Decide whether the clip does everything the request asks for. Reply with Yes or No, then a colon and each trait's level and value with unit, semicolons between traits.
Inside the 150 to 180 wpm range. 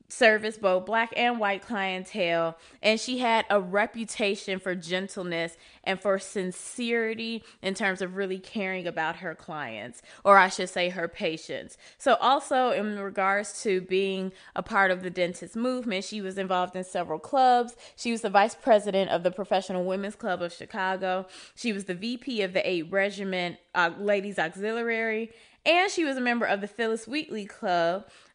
Yes: average, 170 wpm